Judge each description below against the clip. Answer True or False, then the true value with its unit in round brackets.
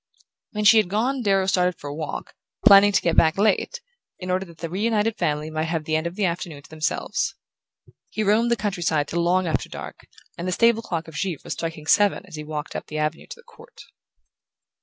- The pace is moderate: False (225 wpm)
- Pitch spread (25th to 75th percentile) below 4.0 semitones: False (4.7 semitones)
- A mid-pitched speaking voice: True (180 Hz)